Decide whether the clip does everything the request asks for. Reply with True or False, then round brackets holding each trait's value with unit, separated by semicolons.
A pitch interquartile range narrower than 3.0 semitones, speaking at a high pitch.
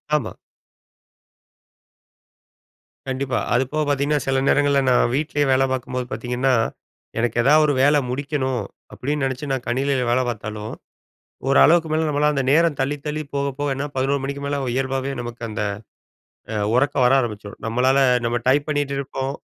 False (2.4 semitones; 135 Hz)